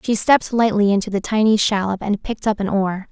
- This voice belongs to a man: No, female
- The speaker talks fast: Yes, fast, 230 wpm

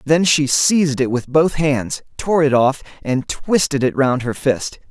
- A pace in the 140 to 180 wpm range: No, average, 195 wpm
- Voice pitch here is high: No, medium, 140 Hz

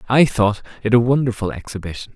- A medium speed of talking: Yes, average, 165 wpm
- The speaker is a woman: No, male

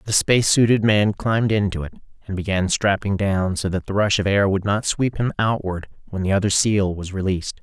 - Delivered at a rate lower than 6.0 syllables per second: Yes, 5.5 syllables/s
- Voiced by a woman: No, male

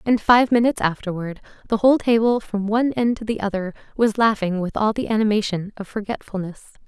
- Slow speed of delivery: No, average, 185 wpm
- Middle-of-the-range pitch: No, high, 215 Hz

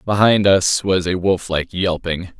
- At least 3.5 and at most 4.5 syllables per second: Yes, 4.4 syllables/s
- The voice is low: Yes, very low, 90 Hz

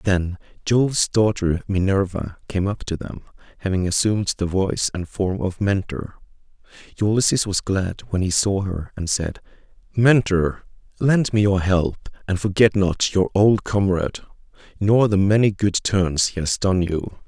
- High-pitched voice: No, very low, 95 Hz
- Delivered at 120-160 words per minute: Yes, average, 155 wpm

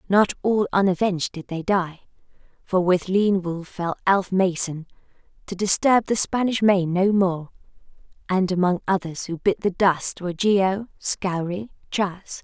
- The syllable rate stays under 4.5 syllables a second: Yes, 4.3 syllables/s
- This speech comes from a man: No, female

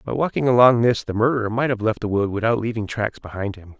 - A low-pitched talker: Yes, low, 110 Hz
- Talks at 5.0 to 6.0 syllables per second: No, 6.3 syllables/s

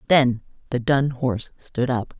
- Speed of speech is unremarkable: Yes, average, 165 wpm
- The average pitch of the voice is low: Yes, low, 125 Hz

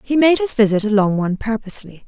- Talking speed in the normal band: No, fast, 230 wpm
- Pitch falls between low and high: No, high, 225 Hz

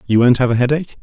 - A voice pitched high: No, low, 130 Hz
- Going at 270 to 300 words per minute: Yes, fast, 295 wpm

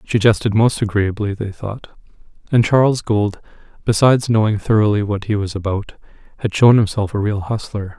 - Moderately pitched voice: No, low, 105 Hz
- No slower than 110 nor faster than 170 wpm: Yes, average, 165 wpm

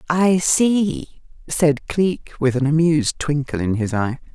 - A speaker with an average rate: Yes, average, 150 wpm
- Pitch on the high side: No, medium, 150 Hz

